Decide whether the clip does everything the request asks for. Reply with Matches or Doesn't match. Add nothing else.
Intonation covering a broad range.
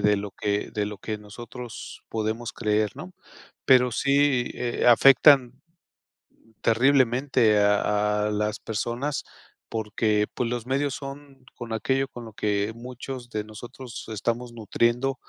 Doesn't match